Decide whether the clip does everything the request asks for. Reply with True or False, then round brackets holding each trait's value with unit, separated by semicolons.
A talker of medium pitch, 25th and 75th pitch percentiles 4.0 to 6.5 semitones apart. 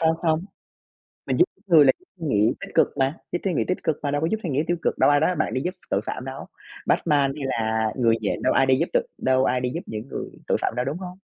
True (145 Hz; 4.4 semitones)